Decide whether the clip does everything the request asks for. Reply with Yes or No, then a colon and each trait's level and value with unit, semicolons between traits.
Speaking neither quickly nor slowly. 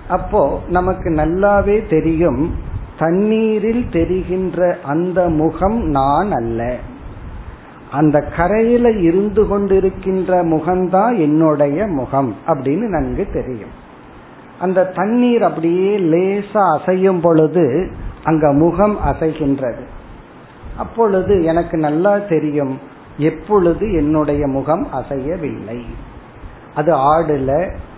Yes: average, 85 wpm